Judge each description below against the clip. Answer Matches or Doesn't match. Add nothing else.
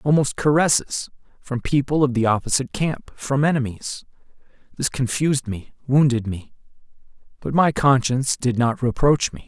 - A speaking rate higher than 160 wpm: Doesn't match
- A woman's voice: Doesn't match